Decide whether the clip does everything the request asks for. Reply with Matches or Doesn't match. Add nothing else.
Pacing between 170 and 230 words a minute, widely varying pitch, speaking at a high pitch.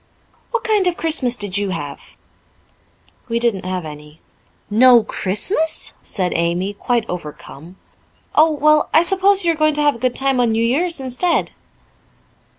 Doesn't match